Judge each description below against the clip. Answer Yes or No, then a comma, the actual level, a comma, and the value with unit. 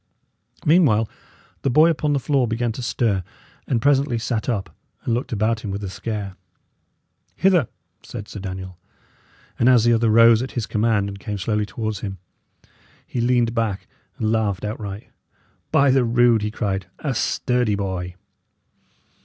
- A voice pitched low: Yes, low, 115 Hz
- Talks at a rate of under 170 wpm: Yes, average, 160 wpm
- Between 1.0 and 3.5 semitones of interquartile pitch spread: Yes, average, 3.1 semitones